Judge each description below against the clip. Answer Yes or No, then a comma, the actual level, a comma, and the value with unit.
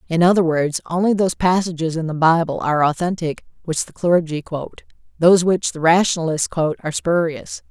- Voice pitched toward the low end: No, medium, 165 Hz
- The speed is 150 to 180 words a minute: Yes, average, 170 wpm